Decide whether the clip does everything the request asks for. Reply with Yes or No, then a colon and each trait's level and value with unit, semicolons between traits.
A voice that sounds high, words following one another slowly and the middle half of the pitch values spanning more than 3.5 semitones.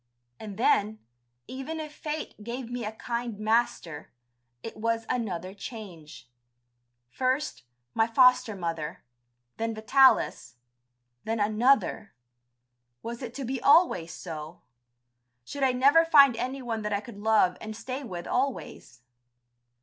Yes: high, 230 Hz; slow, 125 wpm; average, 4.1 semitones